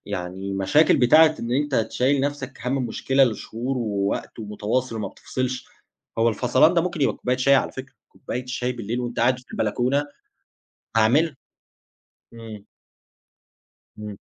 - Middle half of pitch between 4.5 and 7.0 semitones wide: No, average, 3.4 semitones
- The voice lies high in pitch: No, low, 125 Hz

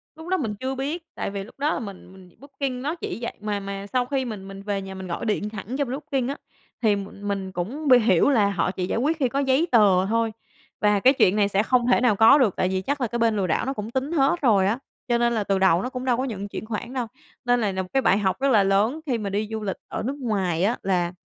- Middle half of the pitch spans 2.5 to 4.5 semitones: No, average, 4.9 semitones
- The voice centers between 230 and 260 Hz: No, high, 220 Hz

